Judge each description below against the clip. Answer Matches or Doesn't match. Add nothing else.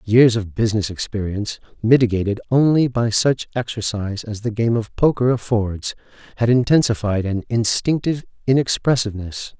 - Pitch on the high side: Doesn't match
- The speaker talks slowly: Matches